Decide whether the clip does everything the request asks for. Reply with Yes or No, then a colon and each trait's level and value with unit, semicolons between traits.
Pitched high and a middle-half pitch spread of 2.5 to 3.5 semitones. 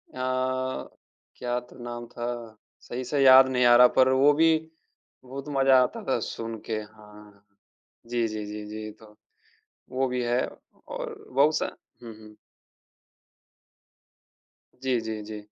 No: low, 120 Hz; average, 3.1 semitones